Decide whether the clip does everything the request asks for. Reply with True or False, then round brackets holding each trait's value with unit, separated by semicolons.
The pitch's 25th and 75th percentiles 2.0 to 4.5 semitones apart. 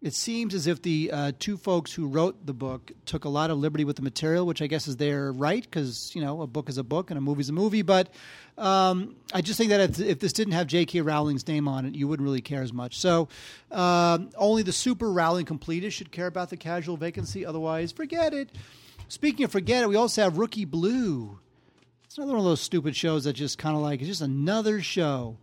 False (4.9 semitones)